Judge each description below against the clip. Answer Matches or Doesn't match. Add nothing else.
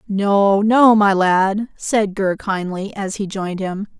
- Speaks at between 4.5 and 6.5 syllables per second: Doesn't match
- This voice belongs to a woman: Matches